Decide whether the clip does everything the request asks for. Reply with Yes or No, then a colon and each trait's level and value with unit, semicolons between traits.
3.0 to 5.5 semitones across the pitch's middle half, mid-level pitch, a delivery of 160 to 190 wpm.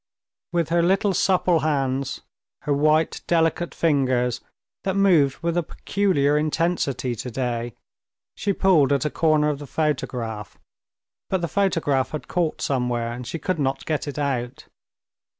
No: average, 4.3 semitones; medium, 150 Hz; average, 145 wpm